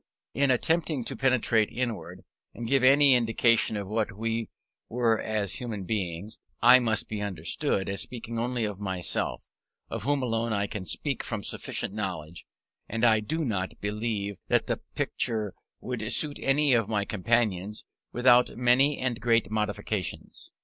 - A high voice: No, low, 115 Hz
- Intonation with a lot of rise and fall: No, average, 3.2 semitones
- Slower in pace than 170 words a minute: Yes, average, 155 wpm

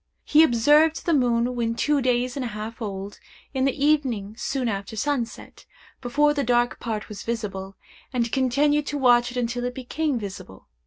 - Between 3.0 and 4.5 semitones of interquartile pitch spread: Yes, average, 3.7 semitones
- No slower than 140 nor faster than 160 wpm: No, average, 175 wpm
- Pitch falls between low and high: No, high, 245 Hz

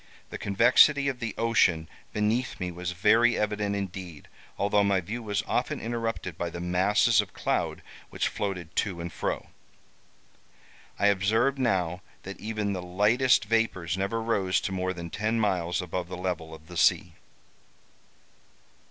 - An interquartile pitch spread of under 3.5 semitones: No, average, 4.0 semitones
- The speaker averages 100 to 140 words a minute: No, average, 150 wpm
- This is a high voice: No, low, 100 Hz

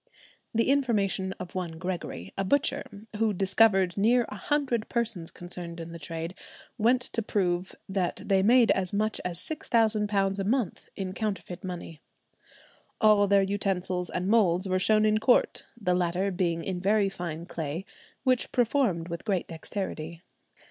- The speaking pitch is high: Yes, high, 195 Hz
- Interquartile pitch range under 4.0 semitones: Yes, average, 3.5 semitones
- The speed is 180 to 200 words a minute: No, average, 155 wpm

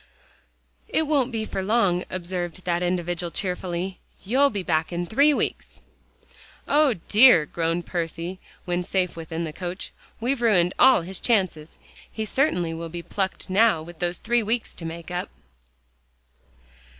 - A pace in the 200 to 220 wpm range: No, average, 150 wpm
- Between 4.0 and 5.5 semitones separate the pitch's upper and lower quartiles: Yes, average, 4.3 semitones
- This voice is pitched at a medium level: Yes, medium, 180 Hz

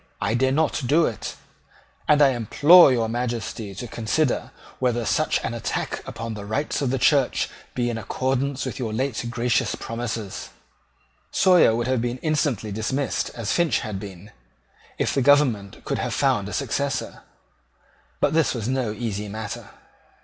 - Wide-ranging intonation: No, average, 3.8 semitones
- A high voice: No, low, 120 Hz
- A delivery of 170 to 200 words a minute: No, average, 160 wpm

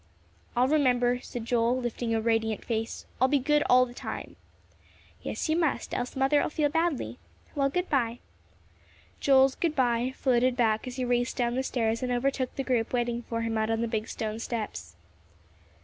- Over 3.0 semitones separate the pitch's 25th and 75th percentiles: No, narrow, 2.6 semitones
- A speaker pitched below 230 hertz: No, high, 245 Hz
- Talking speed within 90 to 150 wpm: No, average, 180 wpm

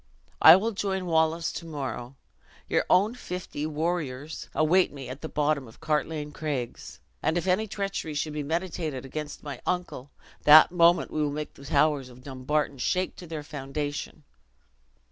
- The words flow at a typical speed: Yes, average, 165 wpm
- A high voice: No, medium, 155 Hz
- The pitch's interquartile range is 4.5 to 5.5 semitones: No, average, 3.3 semitones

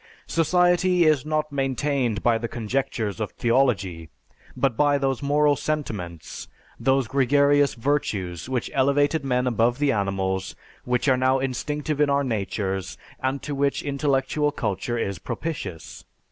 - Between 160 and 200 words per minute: No, slow, 135 wpm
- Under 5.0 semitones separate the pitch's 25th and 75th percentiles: Yes, average, 4.3 semitones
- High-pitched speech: No, low, 135 Hz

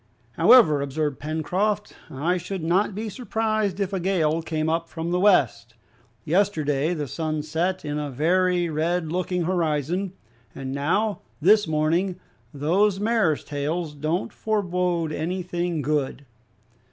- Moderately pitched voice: Yes, medium, 170 Hz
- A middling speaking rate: No, slow, 130 wpm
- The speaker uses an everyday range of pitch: Yes, average, 3.6 semitones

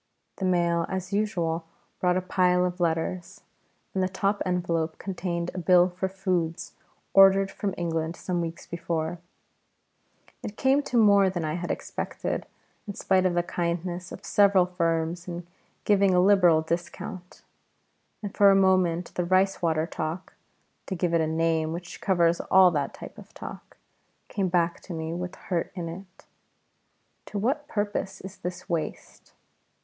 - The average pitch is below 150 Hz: No, medium, 180 Hz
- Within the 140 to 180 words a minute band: Yes, average, 160 wpm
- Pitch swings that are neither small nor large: No, narrow, 2.1 semitones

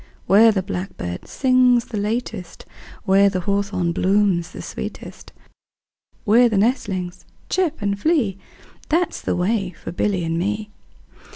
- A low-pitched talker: No, high, 200 Hz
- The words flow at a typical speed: Yes, average, 145 wpm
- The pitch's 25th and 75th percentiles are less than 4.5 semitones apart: Yes, average, 3.8 semitones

